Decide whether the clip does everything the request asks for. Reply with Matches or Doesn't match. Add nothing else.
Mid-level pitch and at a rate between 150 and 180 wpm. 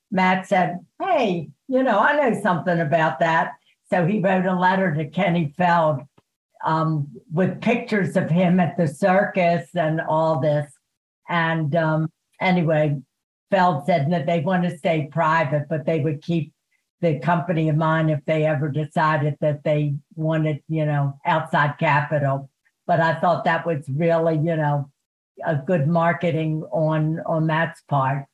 Matches